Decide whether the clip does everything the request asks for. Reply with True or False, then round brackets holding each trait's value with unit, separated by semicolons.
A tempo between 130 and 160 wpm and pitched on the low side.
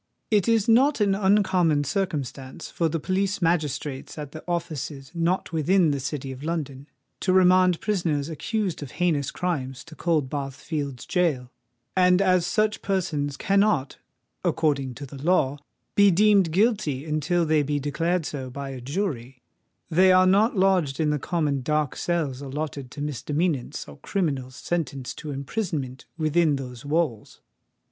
False (150 wpm; 155 Hz)